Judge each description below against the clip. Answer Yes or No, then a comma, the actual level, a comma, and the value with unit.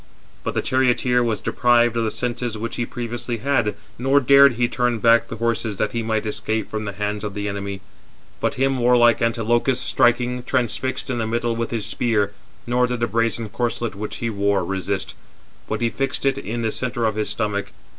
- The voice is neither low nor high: No, low, 115 Hz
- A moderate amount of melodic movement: No, narrow, 2.3 semitones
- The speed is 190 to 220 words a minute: Yes, average, 200 wpm